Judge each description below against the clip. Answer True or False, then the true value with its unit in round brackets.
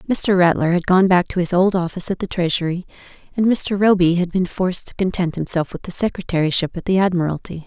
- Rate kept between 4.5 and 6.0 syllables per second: False (6.2 syllables/s)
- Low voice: False (180 Hz)